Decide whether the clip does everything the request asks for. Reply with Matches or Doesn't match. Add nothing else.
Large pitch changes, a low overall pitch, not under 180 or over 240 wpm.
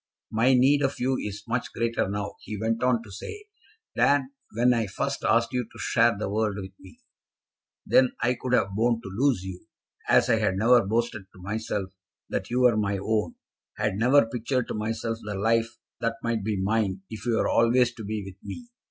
Doesn't match